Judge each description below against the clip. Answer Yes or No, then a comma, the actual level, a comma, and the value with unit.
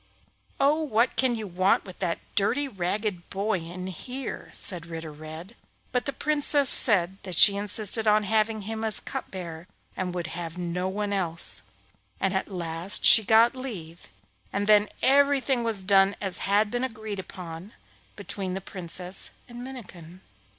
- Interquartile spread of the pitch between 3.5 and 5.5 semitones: Yes, average, 3.9 semitones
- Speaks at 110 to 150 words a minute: No, average, 160 wpm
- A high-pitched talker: Yes, high, 200 Hz